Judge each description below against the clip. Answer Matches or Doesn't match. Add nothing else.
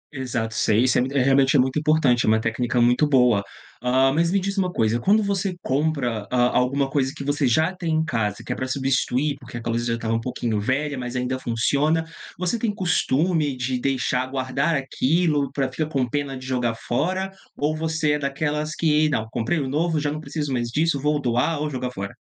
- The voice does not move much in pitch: Doesn't match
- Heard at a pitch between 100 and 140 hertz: Matches